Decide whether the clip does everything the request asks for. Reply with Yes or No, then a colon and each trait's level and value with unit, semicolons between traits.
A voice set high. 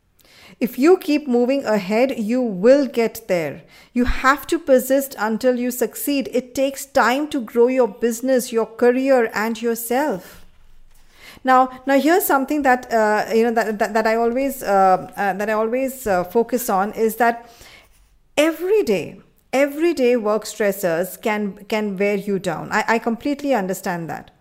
Yes: high, 235 Hz